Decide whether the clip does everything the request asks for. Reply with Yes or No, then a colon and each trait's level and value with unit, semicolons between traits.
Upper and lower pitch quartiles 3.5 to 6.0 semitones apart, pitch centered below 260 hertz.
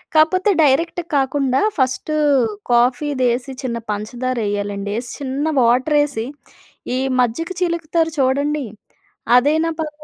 No: average, 3.9 semitones; very high, 270 Hz